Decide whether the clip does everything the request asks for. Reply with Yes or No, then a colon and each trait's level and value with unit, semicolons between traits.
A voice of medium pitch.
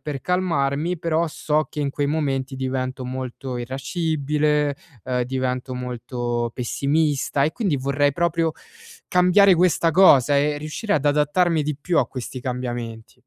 Yes: medium, 145 Hz